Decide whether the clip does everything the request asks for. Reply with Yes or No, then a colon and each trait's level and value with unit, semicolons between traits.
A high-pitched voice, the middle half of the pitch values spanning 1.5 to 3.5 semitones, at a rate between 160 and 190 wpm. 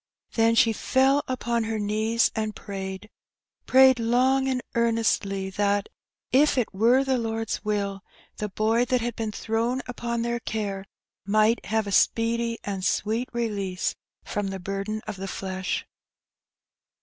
No: high, 225 Hz; average, 2.8 semitones; average, 150 wpm